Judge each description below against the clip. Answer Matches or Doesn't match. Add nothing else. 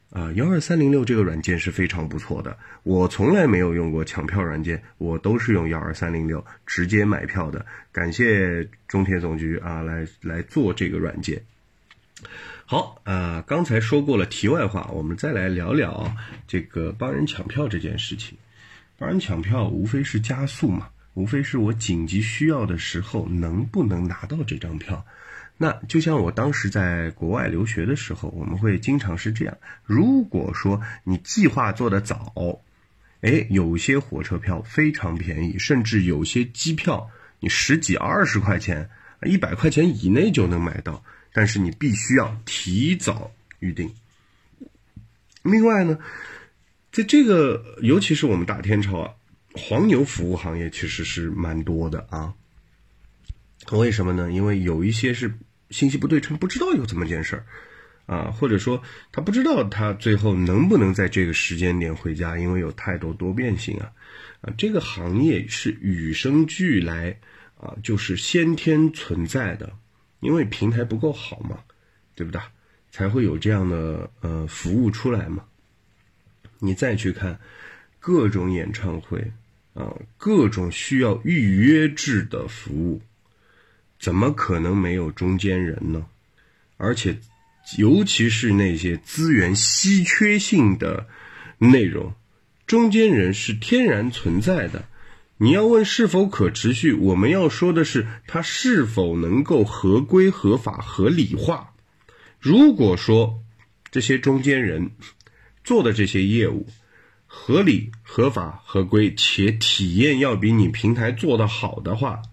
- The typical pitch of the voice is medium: Doesn't match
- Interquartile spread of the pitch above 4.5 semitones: Matches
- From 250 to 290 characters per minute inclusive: Doesn't match